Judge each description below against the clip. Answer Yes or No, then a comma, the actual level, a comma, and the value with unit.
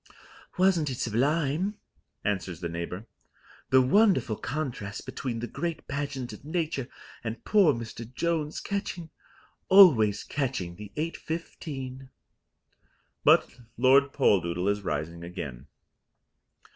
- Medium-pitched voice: No, low, 130 Hz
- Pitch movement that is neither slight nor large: No, wide, 7.4 semitones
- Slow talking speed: Yes, slow, 105 wpm